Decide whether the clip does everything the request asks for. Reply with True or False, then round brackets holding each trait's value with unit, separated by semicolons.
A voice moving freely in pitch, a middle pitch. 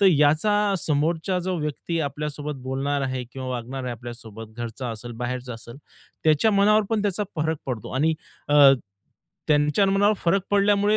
True (6.7 semitones; 150 Hz)